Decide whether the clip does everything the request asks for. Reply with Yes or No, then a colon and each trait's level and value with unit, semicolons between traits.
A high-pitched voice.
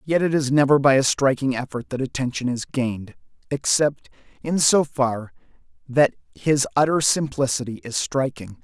No: low, 135 Hz